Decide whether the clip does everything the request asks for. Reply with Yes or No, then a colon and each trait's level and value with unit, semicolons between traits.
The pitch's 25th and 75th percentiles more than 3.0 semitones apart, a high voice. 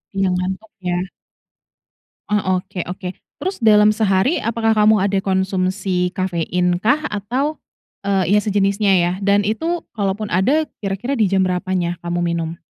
No: narrow, 2.6 semitones; high, 195 Hz